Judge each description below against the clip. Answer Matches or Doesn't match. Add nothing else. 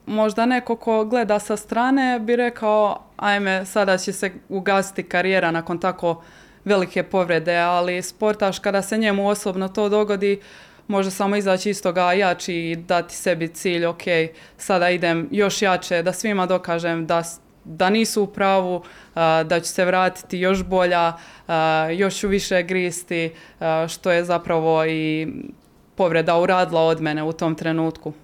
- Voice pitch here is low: Doesn't match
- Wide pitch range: Doesn't match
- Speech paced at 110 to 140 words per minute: Doesn't match